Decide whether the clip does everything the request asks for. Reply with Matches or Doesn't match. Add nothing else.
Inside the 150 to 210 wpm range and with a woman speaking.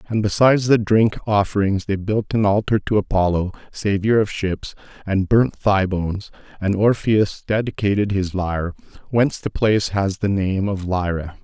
Doesn't match